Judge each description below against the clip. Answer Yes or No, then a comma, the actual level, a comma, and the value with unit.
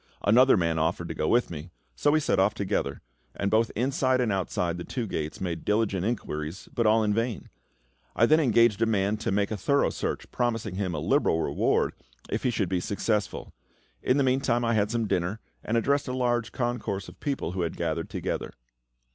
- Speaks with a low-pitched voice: Yes, low, 110 Hz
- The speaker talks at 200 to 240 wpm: Yes, fast, 205 wpm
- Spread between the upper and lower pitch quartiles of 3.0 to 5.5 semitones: Yes, average, 4.5 semitones